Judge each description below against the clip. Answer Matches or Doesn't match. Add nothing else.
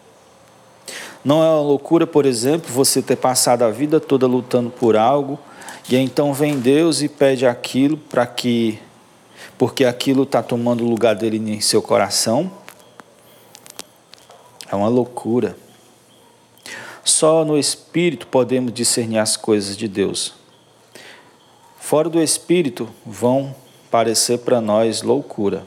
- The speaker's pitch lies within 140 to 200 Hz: Doesn't match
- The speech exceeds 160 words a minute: Doesn't match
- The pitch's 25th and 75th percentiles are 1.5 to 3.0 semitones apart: Doesn't match